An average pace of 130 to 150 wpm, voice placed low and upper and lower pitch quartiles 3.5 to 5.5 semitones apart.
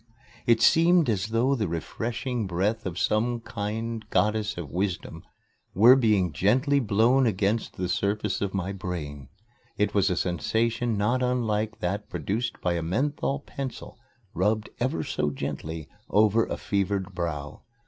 Yes: average, 145 wpm; low, 105 Hz; average, 4.0 semitones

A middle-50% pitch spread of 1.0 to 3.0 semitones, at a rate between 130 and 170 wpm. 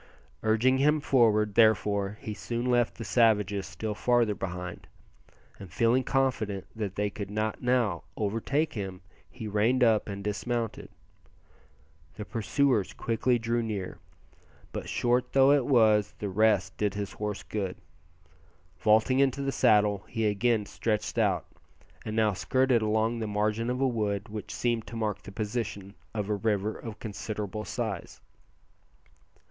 Yes: narrow, 2.5 semitones; average, 145 wpm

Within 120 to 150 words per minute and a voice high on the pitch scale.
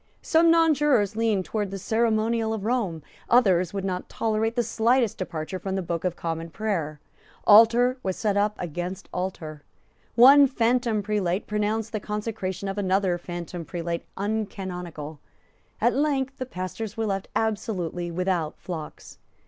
Yes: average, 145 wpm; high, 205 Hz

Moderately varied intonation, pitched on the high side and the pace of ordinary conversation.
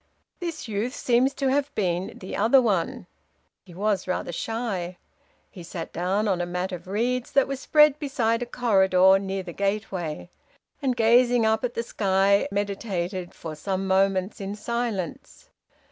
Yes: average, 4.4 semitones; high, 200 Hz; average, 160 wpm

